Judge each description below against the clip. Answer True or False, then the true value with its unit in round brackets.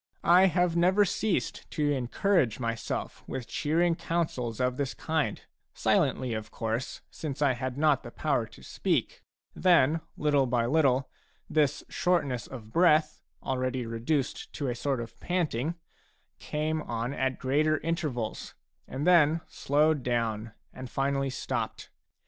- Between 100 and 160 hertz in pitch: True (140 Hz)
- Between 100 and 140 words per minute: True (135 wpm)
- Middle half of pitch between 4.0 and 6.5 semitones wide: True (4.3 semitones)